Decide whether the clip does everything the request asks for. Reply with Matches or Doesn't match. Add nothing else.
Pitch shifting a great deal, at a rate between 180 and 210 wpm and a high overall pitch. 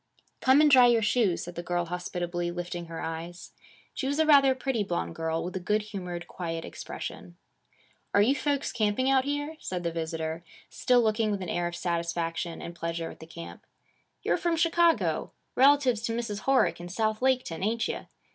Matches